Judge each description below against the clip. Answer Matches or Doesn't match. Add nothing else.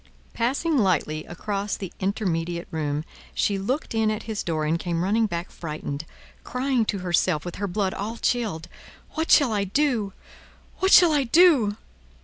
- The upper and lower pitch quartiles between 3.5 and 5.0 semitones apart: Doesn't match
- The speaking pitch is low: Doesn't match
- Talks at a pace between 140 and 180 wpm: Matches